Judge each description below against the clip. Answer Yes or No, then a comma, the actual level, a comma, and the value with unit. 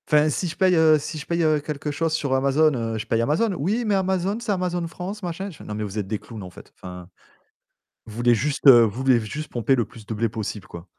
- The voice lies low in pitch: No, medium, 145 Hz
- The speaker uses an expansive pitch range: Yes, wide, 7.2 semitones